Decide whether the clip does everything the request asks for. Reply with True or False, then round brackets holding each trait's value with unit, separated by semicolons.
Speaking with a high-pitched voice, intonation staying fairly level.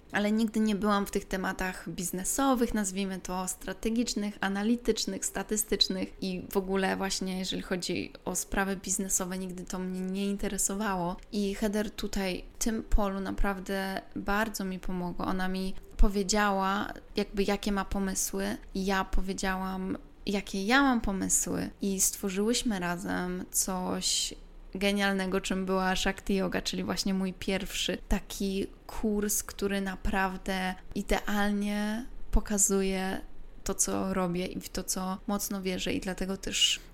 True (195 Hz; 1.6 semitones)